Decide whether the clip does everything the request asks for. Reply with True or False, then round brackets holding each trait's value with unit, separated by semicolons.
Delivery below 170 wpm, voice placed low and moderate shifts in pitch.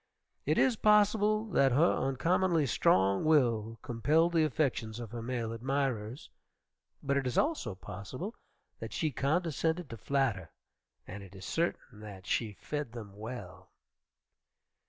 False (135 wpm; 130 Hz; 6.5 semitones)